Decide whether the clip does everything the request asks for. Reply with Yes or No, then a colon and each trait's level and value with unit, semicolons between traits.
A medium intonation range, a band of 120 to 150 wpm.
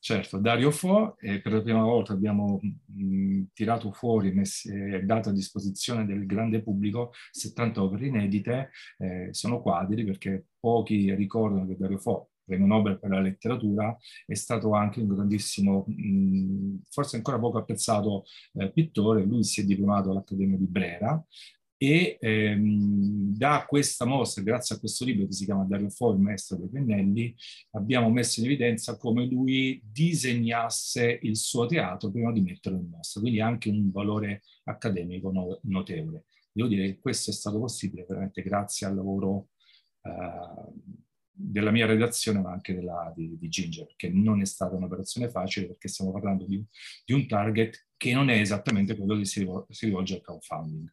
No: average, 3.2 semitones; average, 165 wpm